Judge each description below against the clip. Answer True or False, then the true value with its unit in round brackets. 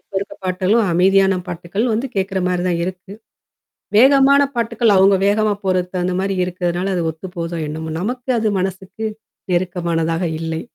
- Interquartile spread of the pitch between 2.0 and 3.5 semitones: True (2.9 semitones)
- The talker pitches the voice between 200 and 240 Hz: False (190 Hz)